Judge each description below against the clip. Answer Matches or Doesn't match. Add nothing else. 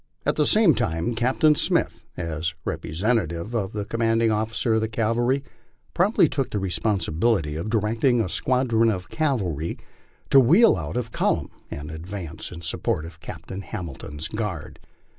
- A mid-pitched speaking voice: Doesn't match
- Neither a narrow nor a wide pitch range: Doesn't match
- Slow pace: Doesn't match